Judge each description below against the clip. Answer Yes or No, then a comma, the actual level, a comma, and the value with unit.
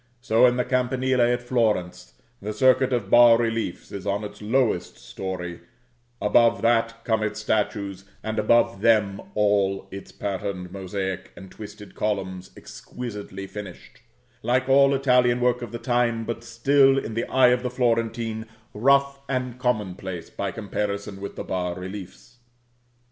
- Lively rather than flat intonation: No, average, 3.8 semitones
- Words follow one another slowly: No, average, 150 wpm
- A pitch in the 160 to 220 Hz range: No, low, 110 Hz